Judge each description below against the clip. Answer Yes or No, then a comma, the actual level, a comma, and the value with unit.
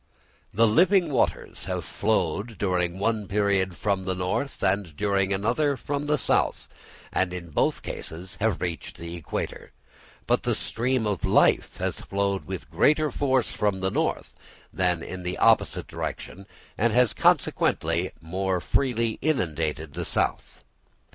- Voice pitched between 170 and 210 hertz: No, low, 100 Hz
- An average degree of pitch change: Yes, average, 4.4 semitones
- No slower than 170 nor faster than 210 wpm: No, average, 145 wpm